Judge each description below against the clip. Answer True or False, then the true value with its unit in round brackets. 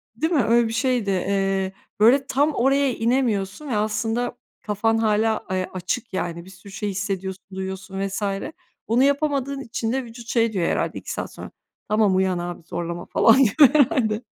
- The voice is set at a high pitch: True (220 Hz)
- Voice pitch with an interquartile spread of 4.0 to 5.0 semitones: True (4.5 semitones)